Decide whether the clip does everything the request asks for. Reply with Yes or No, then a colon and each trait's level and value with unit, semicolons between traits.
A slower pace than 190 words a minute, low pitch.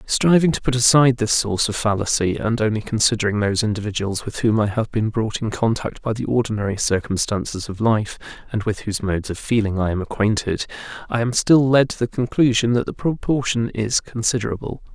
No: average, 195 wpm; low, 110 Hz